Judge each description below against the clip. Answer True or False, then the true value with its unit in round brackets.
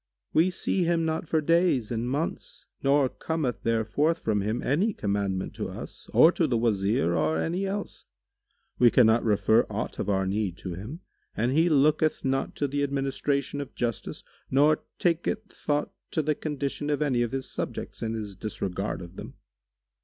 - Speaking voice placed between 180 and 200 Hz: False (135 Hz)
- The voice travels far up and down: True (6.2 semitones)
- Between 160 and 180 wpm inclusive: True (175 wpm)